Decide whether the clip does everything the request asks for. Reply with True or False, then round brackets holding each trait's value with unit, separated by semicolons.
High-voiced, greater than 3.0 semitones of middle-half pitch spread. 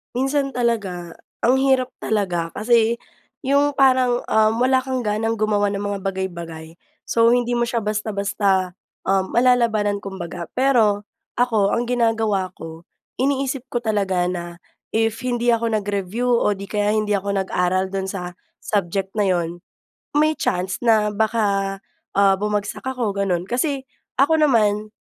True (210 Hz; 3.8 semitones)